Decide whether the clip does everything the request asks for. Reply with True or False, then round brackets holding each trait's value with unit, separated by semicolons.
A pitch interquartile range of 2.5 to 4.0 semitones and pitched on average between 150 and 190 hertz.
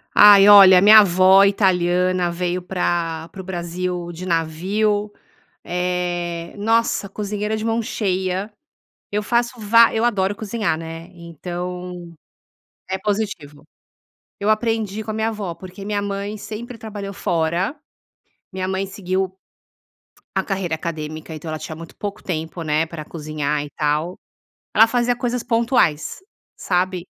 True (3.4 semitones; 185 Hz)